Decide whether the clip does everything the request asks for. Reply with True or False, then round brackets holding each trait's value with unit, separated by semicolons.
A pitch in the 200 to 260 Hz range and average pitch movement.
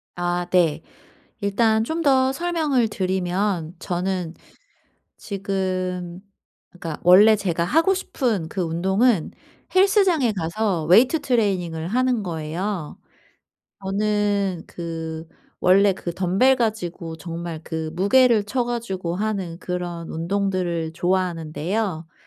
False (190 Hz; 4.3 semitones)